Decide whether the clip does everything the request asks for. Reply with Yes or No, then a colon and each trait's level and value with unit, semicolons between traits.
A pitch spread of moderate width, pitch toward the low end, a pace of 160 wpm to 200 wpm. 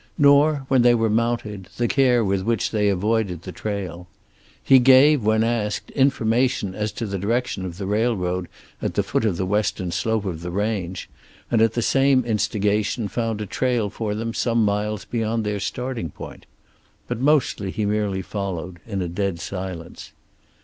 Yes: average, 3.5 semitones; low, 105 Hz; average, 175 wpm